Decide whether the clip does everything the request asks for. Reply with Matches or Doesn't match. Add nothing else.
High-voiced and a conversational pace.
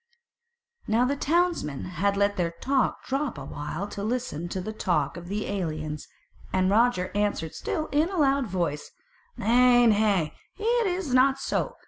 Matches